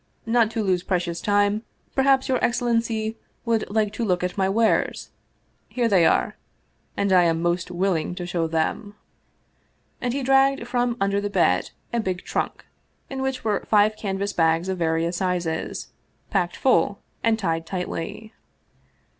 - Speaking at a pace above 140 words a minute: Yes, average, 160 wpm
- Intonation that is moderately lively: Yes, average, 4.4 semitones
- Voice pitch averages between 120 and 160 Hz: No, high, 200 Hz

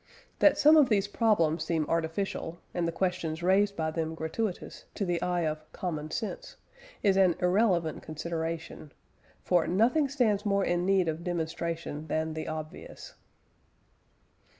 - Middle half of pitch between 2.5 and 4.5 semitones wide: Yes, average, 3.7 semitones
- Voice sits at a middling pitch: Yes, medium, 175 Hz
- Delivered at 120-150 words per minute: Yes, average, 145 wpm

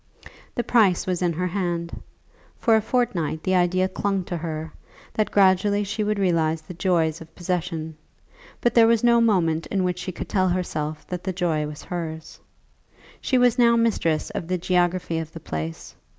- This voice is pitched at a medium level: Yes, medium, 180 Hz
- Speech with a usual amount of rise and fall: Yes, average, 3.7 semitones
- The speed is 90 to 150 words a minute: No, average, 180 wpm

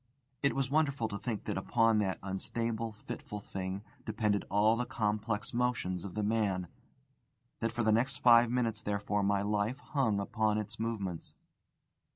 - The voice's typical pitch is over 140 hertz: No, low, 110 Hz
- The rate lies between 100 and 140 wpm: No, average, 160 wpm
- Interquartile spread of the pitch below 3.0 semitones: Yes, narrow, 2.4 semitones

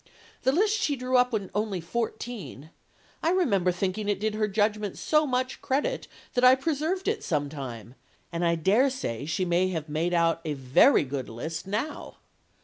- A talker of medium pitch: No, high, 205 Hz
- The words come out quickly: No, average, 180 wpm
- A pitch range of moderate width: No, wide, 7.6 semitones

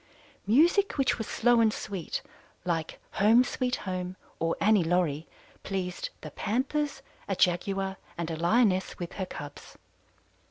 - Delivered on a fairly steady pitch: No, wide, 5.4 semitones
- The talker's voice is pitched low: No, high, 195 Hz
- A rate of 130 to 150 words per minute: Yes, slow, 135 wpm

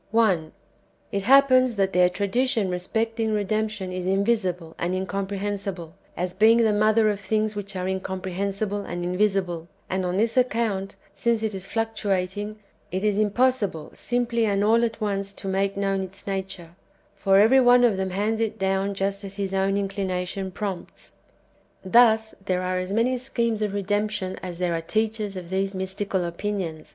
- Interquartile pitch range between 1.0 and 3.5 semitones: Yes, narrow, 2.5 semitones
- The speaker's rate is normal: Yes, average, 165 wpm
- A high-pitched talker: Yes, high, 200 Hz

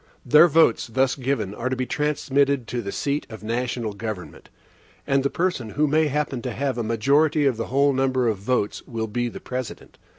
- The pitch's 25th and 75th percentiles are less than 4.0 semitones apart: Yes, average, 3.5 semitones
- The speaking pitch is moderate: No, low, 130 Hz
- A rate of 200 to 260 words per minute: Yes, fast, 205 wpm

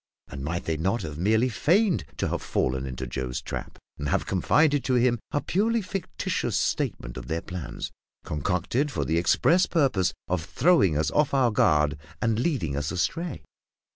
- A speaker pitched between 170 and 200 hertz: No, very low, 95 Hz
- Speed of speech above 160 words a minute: Yes, average, 170 wpm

